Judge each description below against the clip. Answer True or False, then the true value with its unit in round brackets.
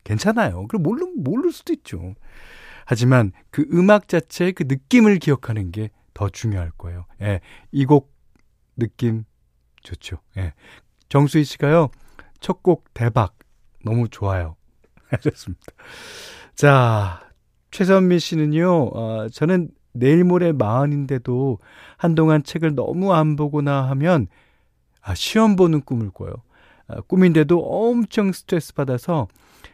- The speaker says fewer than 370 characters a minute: True (240 characters per minute)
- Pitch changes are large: True (8.1 semitones)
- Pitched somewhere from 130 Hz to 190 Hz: True (140 Hz)